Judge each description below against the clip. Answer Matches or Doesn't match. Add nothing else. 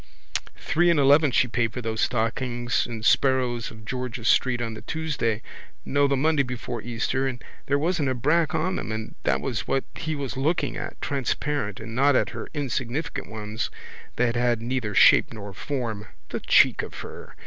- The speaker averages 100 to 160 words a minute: Doesn't match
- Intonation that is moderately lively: Matches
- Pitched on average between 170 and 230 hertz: Doesn't match